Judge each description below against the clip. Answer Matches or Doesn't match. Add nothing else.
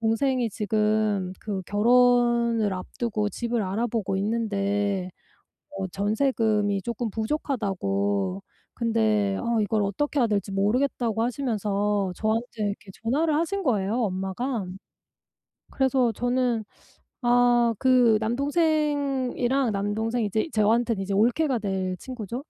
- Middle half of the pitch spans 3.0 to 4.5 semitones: Matches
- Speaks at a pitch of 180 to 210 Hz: Doesn't match